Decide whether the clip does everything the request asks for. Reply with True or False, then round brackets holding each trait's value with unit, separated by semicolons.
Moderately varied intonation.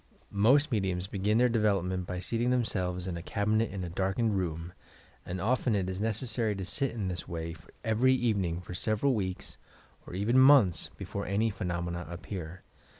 True (4.1 semitones)